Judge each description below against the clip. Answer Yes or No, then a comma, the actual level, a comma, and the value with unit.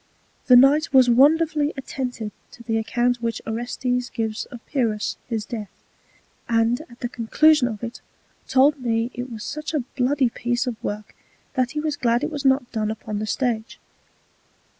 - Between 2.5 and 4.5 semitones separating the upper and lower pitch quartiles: Yes, average, 3.0 semitones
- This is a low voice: No, high, 245 Hz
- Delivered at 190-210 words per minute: No, average, 170 wpm